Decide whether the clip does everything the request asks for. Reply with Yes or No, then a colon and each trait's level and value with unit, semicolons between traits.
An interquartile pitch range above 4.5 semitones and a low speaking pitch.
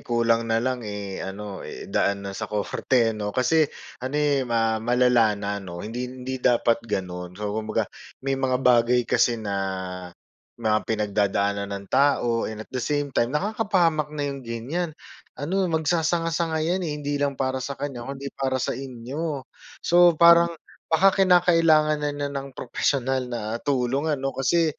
Yes: average, 5.1 semitones; low, 130 Hz